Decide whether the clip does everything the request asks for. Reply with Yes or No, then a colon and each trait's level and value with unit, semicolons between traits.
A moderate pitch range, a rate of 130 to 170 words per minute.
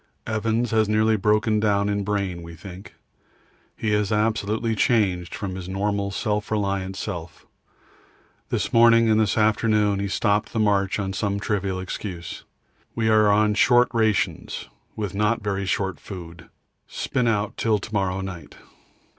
No: narrow, 2.0 semitones; average, 150 wpm